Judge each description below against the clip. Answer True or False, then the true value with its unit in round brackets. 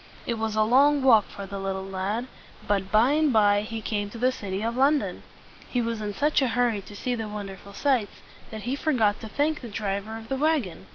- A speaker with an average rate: False (225 wpm)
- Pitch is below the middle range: False (220 Hz)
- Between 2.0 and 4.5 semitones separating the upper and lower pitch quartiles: True (3.8 semitones)